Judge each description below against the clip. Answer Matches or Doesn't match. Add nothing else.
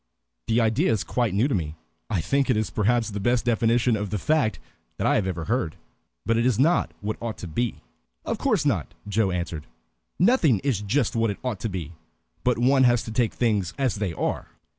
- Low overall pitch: Matches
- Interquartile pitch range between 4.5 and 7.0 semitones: Doesn't match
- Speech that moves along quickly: Matches